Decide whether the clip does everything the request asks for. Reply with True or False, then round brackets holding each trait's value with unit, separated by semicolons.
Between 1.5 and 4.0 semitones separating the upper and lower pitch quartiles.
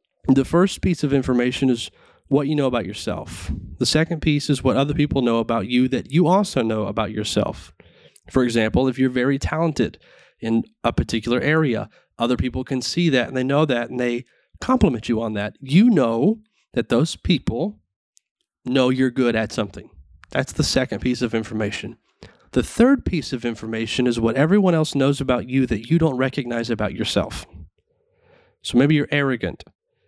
False (4.5 semitones)